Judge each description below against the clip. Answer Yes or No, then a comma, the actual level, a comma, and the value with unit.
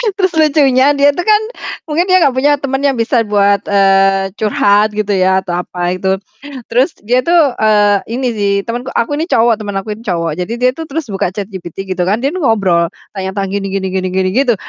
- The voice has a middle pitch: No, high, 215 Hz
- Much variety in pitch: Yes, wide, 5.8 semitones